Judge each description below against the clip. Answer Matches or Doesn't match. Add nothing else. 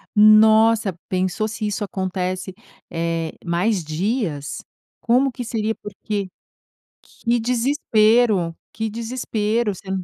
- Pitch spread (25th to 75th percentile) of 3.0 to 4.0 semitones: Matches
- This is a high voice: Matches